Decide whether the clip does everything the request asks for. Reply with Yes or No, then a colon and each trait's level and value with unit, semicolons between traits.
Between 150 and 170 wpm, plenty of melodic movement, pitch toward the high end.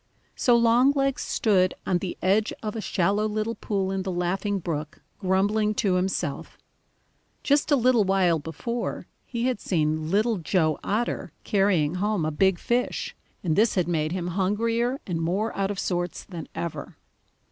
No: average, 160 wpm; average, 3.8 semitones; high, 195 Hz